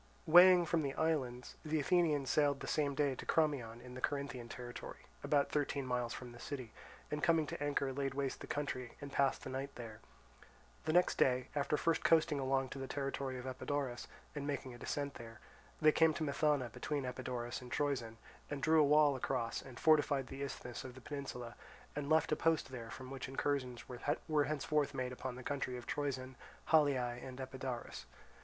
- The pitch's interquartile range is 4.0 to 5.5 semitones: No, narrow, 2.6 semitones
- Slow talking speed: No, average, 190 wpm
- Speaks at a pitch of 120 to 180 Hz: Yes, low, 135 Hz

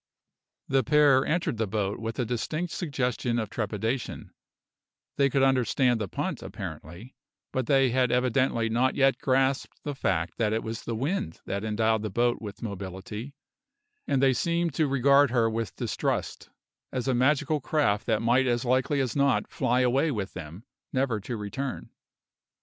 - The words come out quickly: No, average, 165 wpm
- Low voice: Yes, low, 125 Hz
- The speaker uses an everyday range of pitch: Yes, average, 3.6 semitones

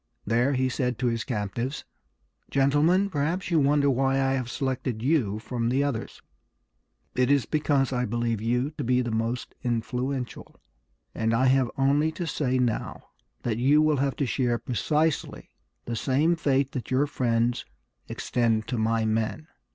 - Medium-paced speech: Yes, average, 160 wpm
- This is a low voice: Yes, low, 130 Hz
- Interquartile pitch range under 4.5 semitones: Yes, average, 3.1 semitones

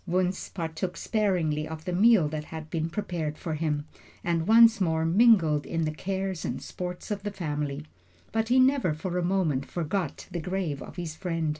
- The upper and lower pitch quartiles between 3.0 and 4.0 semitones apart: Yes, average, 3.6 semitones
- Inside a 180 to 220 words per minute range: Yes, average, 185 wpm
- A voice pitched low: No, medium, 170 Hz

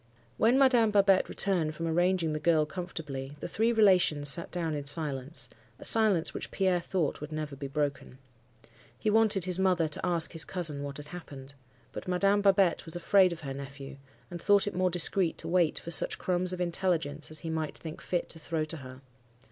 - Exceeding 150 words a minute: Yes, average, 200 wpm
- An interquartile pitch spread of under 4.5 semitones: Yes, average, 3.6 semitones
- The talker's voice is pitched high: No, medium, 170 Hz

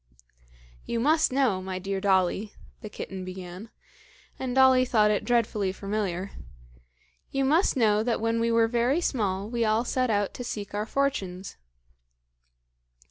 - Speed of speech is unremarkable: Yes, average, 145 wpm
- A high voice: Yes, high, 215 Hz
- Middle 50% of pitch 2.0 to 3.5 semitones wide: No, average, 4.1 semitones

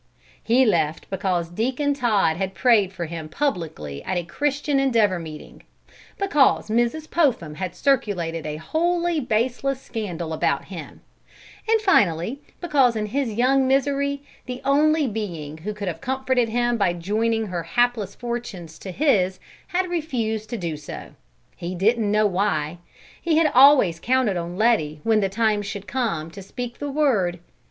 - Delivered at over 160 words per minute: No, average, 155 wpm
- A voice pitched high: Yes, high, 220 Hz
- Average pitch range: No, wide, 7.1 semitones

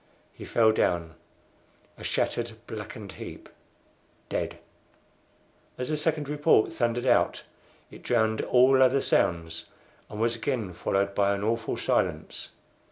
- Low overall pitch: Yes, low, 115 Hz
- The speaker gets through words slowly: Yes, slow, 125 wpm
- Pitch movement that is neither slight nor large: Yes, average, 4.3 semitones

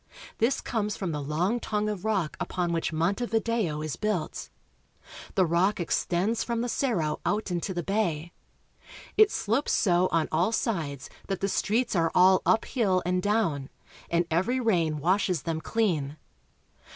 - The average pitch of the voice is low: No, medium, 185 Hz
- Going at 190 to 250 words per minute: No, average, 155 wpm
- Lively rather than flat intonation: No, average, 4.8 semitones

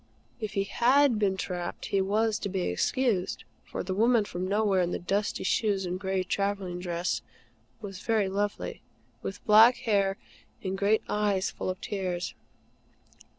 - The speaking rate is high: No, average, 155 wpm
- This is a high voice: Yes, high, 195 Hz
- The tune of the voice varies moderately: No, narrow, 2.3 semitones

